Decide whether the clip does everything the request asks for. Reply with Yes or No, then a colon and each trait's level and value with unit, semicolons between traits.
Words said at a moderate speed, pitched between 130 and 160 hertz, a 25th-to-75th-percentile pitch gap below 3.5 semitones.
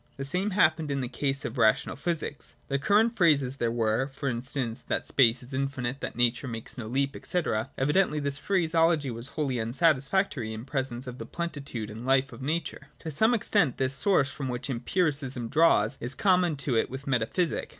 No: average, 195 wpm; low, 135 Hz; average, 4.4 semitones